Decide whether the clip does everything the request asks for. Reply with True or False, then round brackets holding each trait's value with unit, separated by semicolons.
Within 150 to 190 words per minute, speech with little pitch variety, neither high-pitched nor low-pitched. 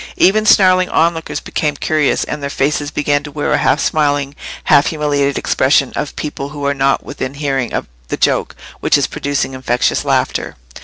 True (175 wpm; 1.5 semitones; 145 Hz)